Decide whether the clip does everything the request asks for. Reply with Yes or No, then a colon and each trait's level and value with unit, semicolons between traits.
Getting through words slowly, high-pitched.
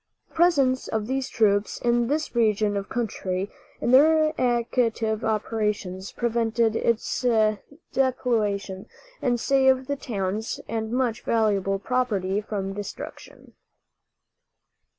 Yes: slow, 110 wpm; high, 225 Hz